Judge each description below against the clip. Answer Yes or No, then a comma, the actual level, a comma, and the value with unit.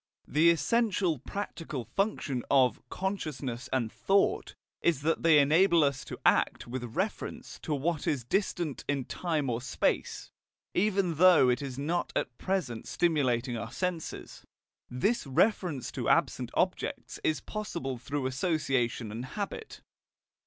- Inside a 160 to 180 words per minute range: No, slow, 135 wpm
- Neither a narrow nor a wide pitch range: No, wide, 5.9 semitones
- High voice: No, medium, 150 Hz